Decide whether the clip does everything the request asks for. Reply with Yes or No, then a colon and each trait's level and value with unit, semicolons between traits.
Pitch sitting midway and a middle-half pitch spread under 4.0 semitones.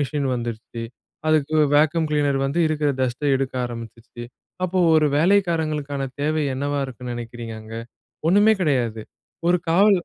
No: medium, 145 Hz; average, 4.5 semitones